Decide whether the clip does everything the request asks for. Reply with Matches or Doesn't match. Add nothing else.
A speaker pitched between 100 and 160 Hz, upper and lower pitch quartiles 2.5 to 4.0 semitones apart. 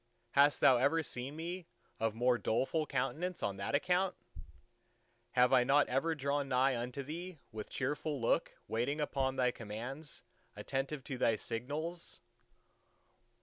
Matches